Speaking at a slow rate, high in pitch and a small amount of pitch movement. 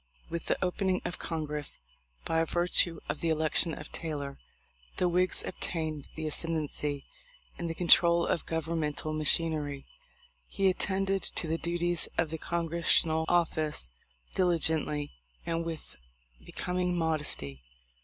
No: slow, 130 wpm; medium, 165 Hz; narrow, 1.9 semitones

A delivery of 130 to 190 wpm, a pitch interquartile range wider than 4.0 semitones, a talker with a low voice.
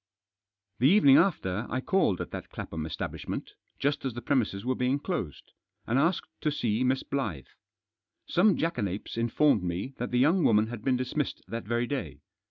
Yes: average, 180 wpm; average, 5.1 semitones; low, 125 Hz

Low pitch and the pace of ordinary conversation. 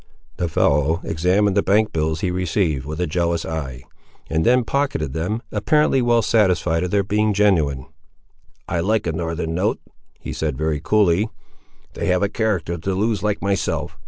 Yes: very low, 90 Hz; average, 170 wpm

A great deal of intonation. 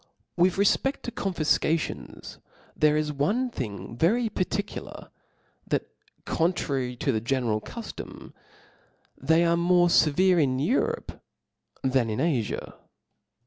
Yes: wide, 5.9 semitones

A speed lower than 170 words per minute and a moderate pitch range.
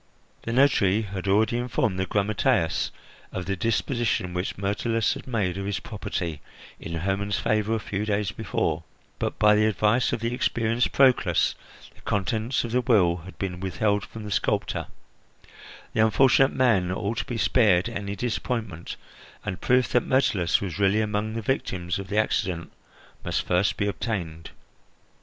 Yes: average, 160 wpm; average, 3.5 semitones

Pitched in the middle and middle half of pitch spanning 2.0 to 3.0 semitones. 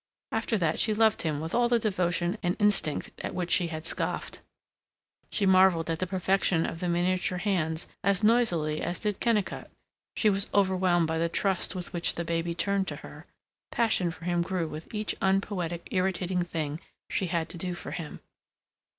Yes: medium, 180 Hz; average, 2.7 semitones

